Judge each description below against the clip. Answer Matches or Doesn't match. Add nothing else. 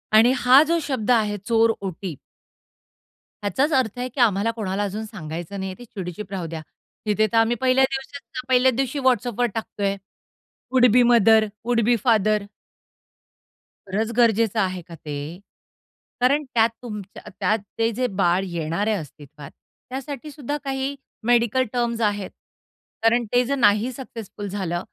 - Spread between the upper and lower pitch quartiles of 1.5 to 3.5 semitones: Doesn't match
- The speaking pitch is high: Matches